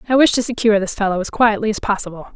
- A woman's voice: Yes, female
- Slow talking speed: No, fast, 255 wpm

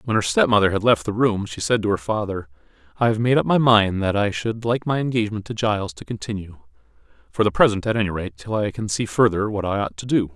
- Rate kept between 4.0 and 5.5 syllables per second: No, 6.2 syllables/s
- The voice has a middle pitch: No, low, 105 Hz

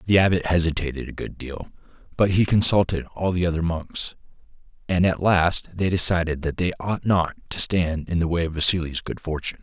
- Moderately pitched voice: No, very low, 85 Hz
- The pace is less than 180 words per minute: No, average, 195 wpm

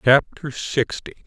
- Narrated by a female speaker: No, male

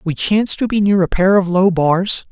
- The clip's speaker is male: Yes, male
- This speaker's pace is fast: Yes, fast, 260 wpm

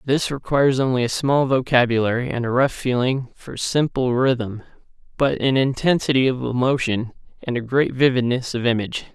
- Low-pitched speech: Yes, low, 125 Hz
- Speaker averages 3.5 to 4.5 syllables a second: No, 5.2 syllables/s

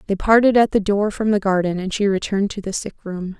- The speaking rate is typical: No, fast, 265 wpm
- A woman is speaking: Yes, female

